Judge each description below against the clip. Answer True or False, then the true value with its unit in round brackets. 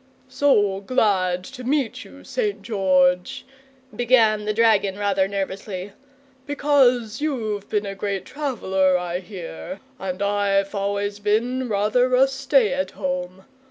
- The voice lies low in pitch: False (205 Hz)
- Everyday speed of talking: False (125 wpm)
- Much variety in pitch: False (4.6 semitones)